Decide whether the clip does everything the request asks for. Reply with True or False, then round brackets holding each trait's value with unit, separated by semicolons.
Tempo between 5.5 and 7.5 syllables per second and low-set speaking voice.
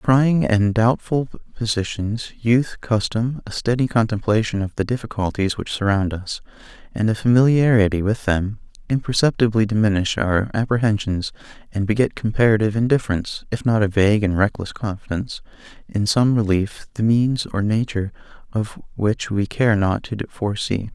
False (5.2 syllables/s; 110 Hz)